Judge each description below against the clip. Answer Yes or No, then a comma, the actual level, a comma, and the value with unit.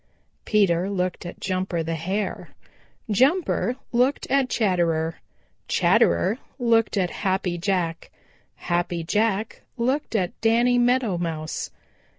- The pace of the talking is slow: Yes, slow, 110 wpm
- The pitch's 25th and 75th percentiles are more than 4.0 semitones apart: Yes, average, 5.2 semitones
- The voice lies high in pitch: Yes, high, 195 Hz